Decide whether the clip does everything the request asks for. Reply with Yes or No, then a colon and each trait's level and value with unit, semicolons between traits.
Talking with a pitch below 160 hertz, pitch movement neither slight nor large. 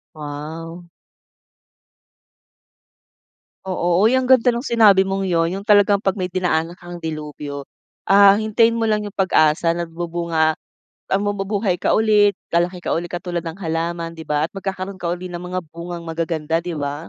No: medium, 175 Hz; average, 3.2 semitones